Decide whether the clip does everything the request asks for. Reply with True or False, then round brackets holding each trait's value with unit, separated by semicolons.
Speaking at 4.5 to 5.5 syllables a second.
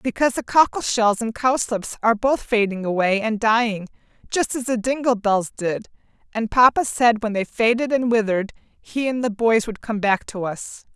True (5.0 syllables/s)